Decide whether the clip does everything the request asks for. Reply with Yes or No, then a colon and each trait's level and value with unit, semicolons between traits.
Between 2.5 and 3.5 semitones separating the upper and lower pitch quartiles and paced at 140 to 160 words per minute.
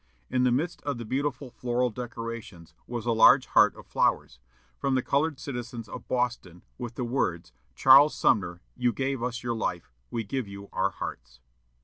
No: average, 2.9 semitones; average, 175 wpm